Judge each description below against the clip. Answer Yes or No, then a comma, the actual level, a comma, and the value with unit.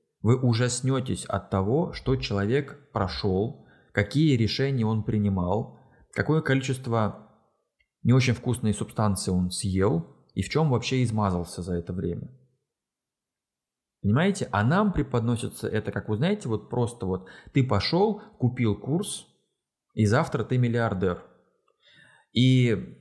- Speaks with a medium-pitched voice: No, low, 120 Hz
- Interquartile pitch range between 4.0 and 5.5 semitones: Yes, average, 4.7 semitones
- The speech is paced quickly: No, average, 125 wpm